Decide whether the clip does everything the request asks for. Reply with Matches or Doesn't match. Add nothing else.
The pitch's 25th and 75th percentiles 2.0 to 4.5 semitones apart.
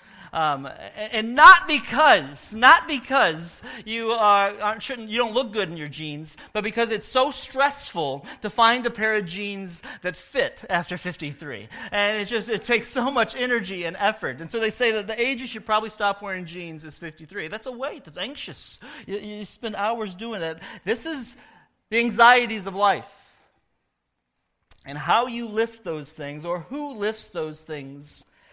Doesn't match